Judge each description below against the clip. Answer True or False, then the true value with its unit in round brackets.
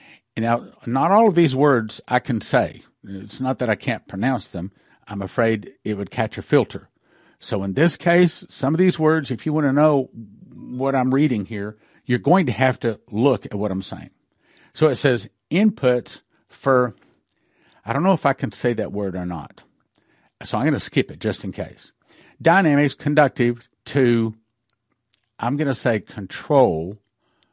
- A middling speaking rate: True (180 wpm)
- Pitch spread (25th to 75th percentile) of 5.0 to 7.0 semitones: True (5.4 semitones)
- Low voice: True (125 Hz)